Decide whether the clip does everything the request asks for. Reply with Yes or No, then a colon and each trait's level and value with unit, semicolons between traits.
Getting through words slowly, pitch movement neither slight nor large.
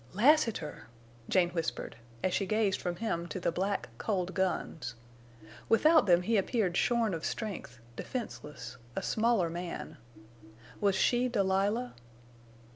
Yes: slow, 125 wpm; average, 4.6 semitones